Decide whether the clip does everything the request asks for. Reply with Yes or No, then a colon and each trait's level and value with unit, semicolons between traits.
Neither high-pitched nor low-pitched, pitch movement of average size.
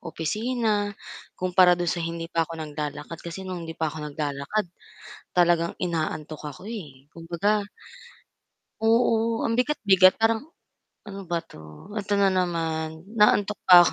Yes: medium, 175 Hz; average, 4.4 semitones